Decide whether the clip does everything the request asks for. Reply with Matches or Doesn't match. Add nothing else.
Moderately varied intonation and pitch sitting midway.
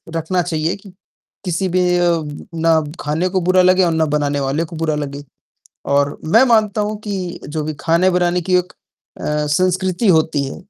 Matches